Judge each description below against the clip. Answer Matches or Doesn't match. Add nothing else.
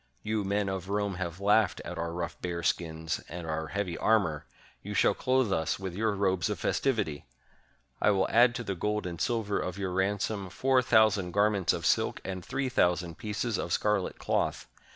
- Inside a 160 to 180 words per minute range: Doesn't match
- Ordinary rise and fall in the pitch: Matches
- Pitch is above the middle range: Doesn't match